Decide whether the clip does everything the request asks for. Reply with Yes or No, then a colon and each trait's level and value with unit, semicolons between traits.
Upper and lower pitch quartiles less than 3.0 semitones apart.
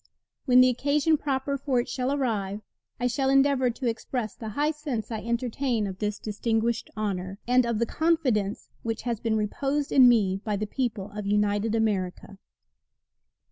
No: average, 4.1 semitones